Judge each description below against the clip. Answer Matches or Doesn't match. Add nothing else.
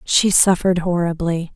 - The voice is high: Doesn't match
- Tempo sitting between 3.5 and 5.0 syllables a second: Matches